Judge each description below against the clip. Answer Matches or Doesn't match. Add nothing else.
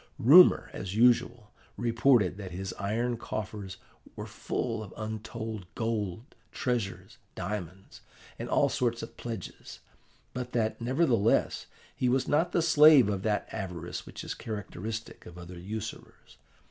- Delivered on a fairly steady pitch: Doesn't match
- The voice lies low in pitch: Matches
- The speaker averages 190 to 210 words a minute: Doesn't match